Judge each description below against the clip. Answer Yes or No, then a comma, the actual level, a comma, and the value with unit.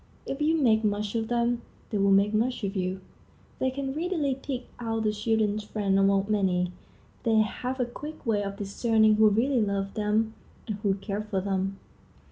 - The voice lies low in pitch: No, high, 215 Hz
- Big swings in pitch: No, average, 3.2 semitones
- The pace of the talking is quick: No, average, 185 wpm